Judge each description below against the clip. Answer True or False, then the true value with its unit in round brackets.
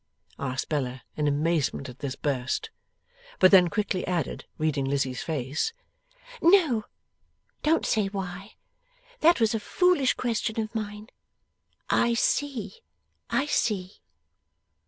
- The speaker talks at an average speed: False (115 wpm)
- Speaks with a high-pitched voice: True (195 Hz)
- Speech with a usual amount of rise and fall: False (8.1 semitones)